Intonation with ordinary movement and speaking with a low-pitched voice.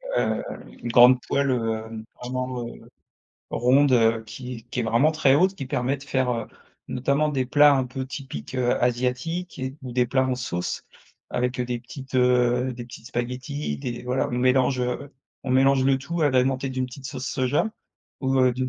No: narrow, 1.6 semitones; low, 130 Hz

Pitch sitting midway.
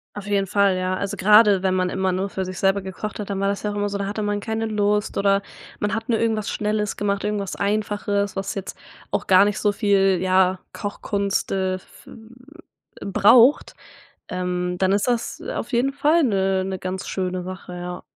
No: high, 200 Hz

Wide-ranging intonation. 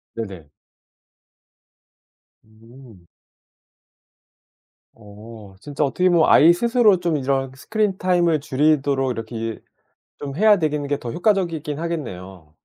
Yes: wide, 7.0 semitones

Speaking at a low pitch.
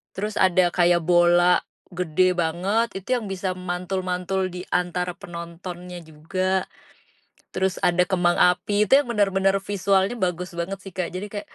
No: medium, 185 Hz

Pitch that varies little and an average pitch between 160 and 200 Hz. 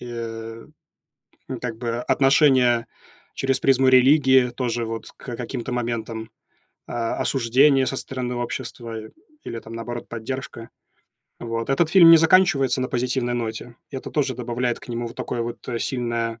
No: narrow, 2.2 semitones; low, 120 Hz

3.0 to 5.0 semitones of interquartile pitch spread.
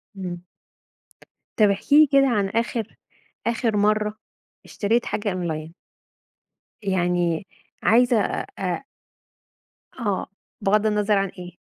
Yes: average, 3.4 semitones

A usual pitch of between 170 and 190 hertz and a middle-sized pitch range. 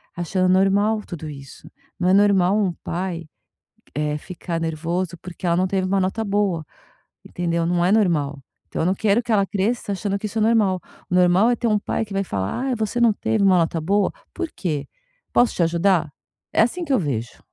Yes: medium, 185 Hz; average, 3.5 semitones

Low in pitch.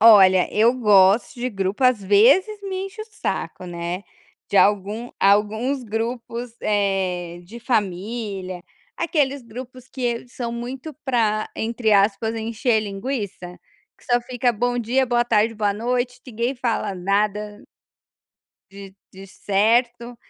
No: high, 225 Hz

